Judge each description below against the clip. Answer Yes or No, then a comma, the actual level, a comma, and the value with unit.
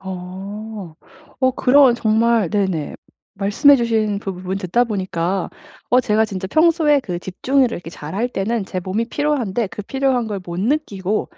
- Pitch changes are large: No, average, 4.4 semitones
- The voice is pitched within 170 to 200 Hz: No, high, 210 Hz